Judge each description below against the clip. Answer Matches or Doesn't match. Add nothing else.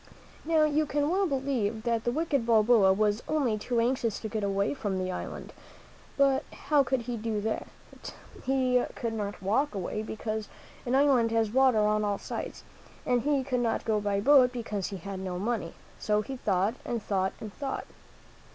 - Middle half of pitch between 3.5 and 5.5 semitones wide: Matches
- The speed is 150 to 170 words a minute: Doesn't match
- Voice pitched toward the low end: Doesn't match